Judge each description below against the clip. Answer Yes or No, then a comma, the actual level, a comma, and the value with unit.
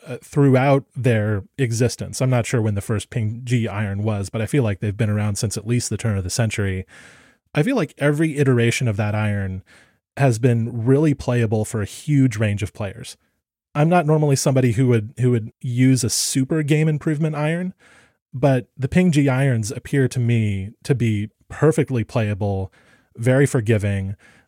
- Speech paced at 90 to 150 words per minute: No, average, 180 wpm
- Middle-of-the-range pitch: No, low, 120 Hz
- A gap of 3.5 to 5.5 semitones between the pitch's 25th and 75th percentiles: Yes, average, 4.4 semitones